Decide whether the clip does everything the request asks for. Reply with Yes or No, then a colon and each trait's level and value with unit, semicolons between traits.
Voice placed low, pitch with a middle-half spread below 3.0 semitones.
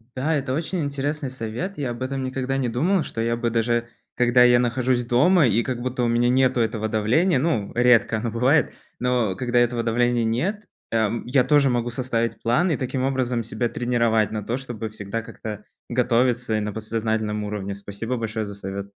Yes: low, 120 Hz; narrow, 2.4 semitones